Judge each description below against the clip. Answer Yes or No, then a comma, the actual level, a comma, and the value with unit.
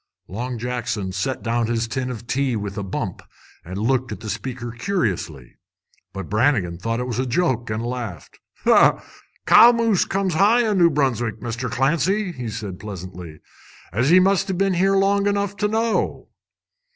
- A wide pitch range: Yes, wide, 9.0 semitones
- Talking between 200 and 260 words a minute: No, average, 170 wpm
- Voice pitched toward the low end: Yes, low, 125 Hz